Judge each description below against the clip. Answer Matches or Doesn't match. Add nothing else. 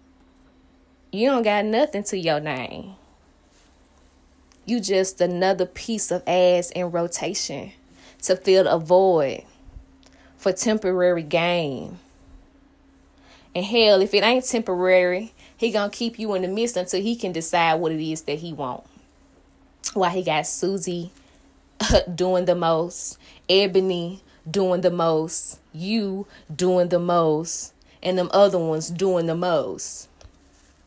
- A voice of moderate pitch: Matches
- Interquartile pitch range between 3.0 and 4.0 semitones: Doesn't match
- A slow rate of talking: Matches